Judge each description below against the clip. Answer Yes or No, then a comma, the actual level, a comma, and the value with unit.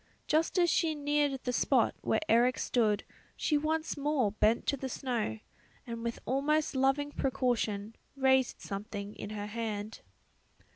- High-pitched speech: Yes, very high, 255 Hz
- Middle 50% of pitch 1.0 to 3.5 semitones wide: No, average, 4.8 semitones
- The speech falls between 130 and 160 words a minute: Yes, average, 145 wpm